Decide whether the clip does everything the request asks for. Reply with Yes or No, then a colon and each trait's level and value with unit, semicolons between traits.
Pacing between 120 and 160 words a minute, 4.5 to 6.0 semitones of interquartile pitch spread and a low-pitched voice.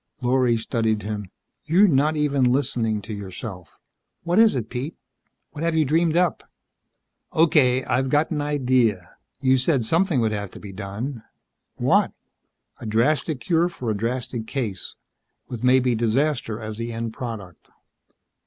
Yes: average, 150 wpm; average, 5.0 semitones; low, 125 Hz